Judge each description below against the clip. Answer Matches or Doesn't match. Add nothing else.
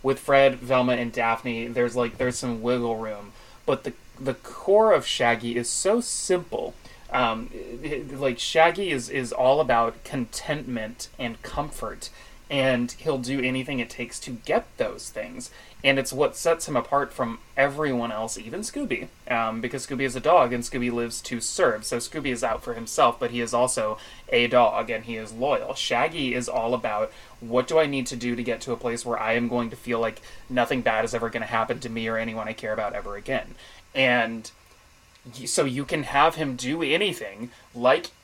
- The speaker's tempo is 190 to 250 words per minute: Matches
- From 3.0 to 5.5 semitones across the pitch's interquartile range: Doesn't match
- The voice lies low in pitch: Matches